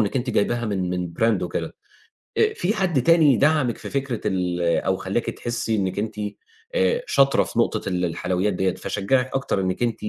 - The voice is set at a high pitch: No, low, 110 Hz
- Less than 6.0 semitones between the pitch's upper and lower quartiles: No, wide, 6.3 semitones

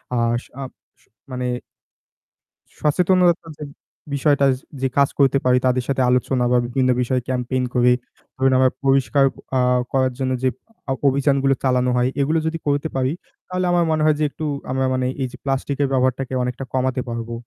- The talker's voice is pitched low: Yes, low, 130 Hz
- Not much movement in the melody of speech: Yes, narrow, 1.8 semitones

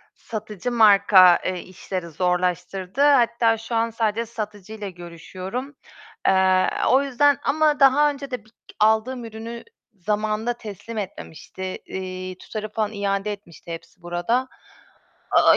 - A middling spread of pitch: Yes, average, 4.1 semitones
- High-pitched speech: Yes, high, 215 Hz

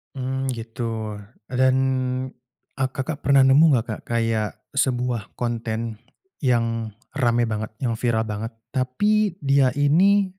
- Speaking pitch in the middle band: No, low, 125 Hz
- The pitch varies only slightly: No, average, 3.0 semitones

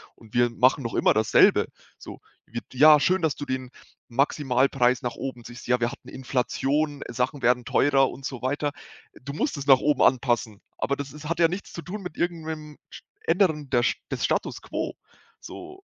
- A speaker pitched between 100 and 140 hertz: Yes, low, 135 Hz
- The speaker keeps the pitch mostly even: No, average, 3.5 semitones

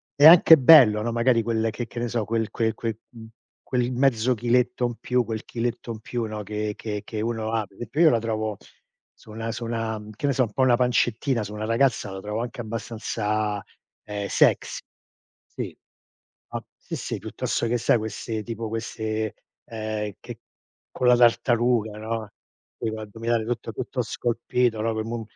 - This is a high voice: No, low, 115 Hz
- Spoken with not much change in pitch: Yes, narrow, 1.8 semitones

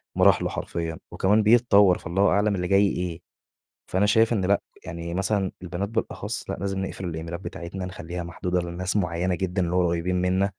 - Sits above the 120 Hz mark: No, very low, 90 Hz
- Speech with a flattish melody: Yes, narrow, 2.3 semitones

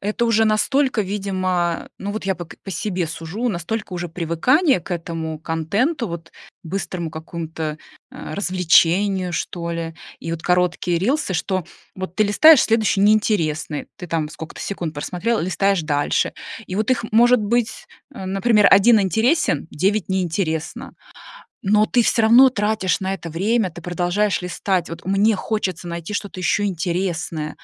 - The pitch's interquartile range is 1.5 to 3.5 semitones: No, average, 4.2 semitones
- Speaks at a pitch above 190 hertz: No, medium, 185 Hz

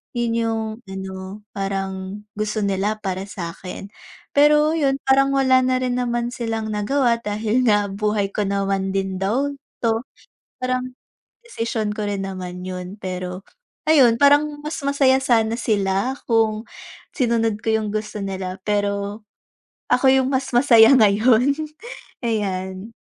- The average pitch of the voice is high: Yes, high, 215 Hz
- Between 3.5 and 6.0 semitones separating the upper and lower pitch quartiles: Yes, average, 4.3 semitones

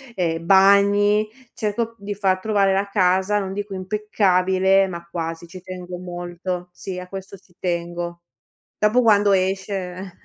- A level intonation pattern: Yes, narrow, 2.1 semitones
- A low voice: No, high, 190 Hz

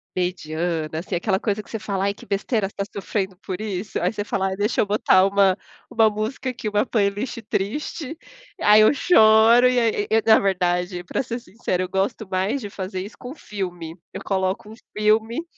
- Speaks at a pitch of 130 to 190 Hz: No, high, 205 Hz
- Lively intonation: No, average, 2.7 semitones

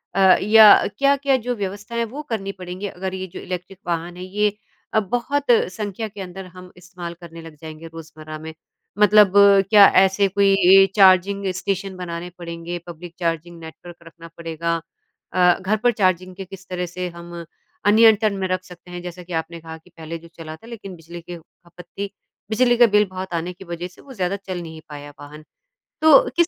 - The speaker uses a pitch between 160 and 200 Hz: Yes, medium, 185 Hz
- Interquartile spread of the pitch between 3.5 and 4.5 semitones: No, average, 2.9 semitones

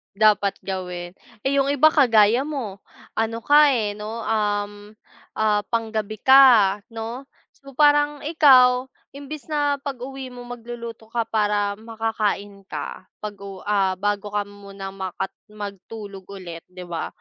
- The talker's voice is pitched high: Yes, high, 220 Hz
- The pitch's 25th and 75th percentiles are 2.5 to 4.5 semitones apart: Yes, average, 4.1 semitones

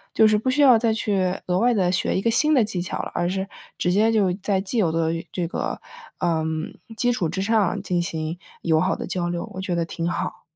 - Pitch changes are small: No, average, 4.1 semitones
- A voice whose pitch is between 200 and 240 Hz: No, high, 190 Hz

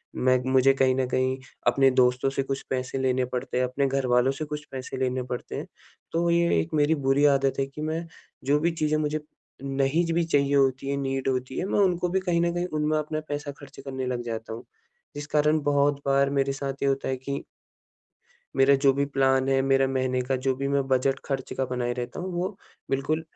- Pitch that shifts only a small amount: Yes, narrow, 2.3 semitones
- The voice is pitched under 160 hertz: Yes, low, 135 Hz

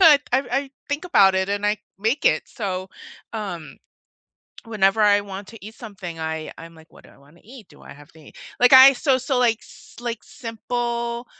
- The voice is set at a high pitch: Yes, high, 215 Hz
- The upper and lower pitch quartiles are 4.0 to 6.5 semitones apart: Yes, average, 4.5 semitones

